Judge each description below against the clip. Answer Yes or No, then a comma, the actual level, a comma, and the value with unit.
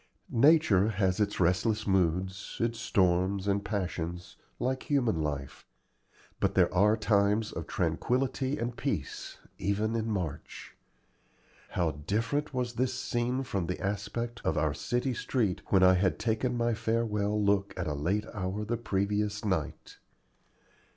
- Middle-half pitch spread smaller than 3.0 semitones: No, average, 4.0 semitones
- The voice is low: Yes, low, 105 Hz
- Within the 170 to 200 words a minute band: No, average, 140 wpm